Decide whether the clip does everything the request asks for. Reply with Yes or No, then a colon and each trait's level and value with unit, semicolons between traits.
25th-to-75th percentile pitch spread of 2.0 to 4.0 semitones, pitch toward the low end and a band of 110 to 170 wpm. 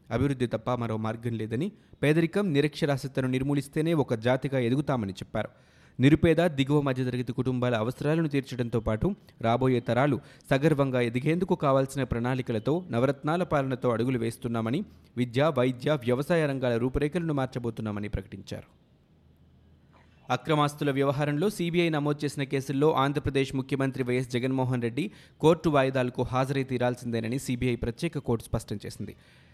Yes: average, 3.4 semitones; low, 130 Hz; average, 115 wpm